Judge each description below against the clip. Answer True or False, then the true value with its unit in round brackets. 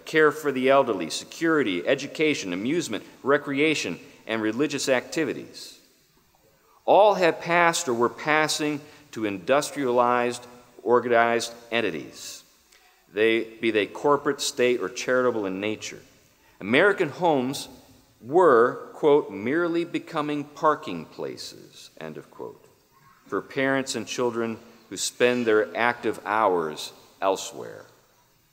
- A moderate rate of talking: False (105 wpm)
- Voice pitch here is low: True (130 Hz)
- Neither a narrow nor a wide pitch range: True (4.3 semitones)